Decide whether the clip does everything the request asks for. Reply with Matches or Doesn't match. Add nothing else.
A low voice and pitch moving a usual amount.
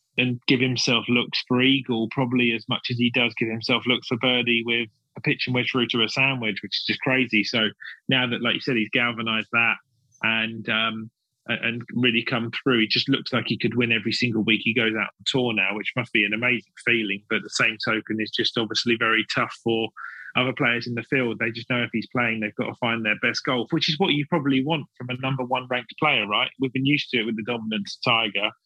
Doesn't match